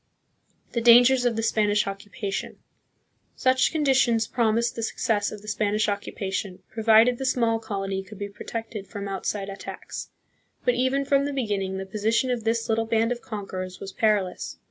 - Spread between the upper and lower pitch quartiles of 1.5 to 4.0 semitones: Yes, average, 2.9 semitones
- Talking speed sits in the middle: Yes, average, 170 wpm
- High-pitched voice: Yes, high, 220 Hz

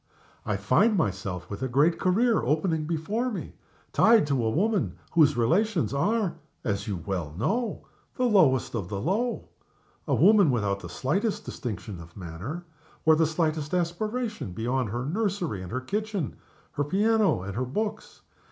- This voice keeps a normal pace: Yes, average, 160 wpm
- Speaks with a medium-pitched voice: Yes, medium, 155 Hz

